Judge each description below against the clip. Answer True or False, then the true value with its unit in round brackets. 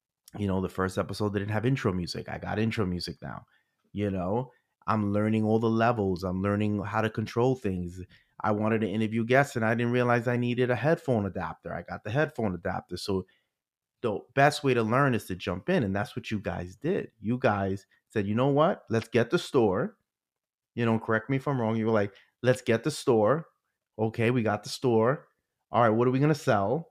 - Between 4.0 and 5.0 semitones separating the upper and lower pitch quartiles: False (3.6 semitones)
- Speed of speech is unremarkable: False (220 wpm)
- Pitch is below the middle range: True (110 Hz)